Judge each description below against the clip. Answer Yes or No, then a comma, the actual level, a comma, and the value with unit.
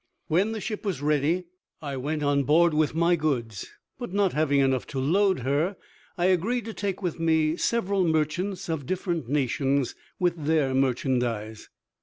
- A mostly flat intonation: No, average, 4.8 semitones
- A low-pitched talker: No, medium, 155 Hz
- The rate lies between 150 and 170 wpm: Yes, average, 165 wpm